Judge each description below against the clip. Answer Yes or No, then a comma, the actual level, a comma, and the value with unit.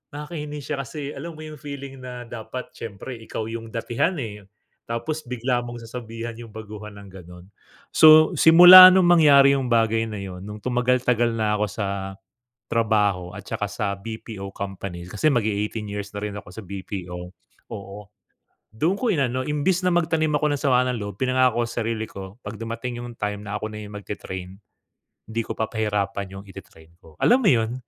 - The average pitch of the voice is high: No, low, 115 Hz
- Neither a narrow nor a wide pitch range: Yes, average, 4.4 semitones